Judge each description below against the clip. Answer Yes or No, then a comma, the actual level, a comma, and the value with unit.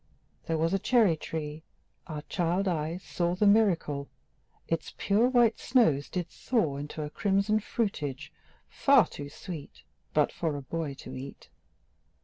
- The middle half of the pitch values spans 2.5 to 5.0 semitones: No, wide, 5.4 semitones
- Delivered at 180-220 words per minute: No, average, 145 wpm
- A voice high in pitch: No, medium, 170 Hz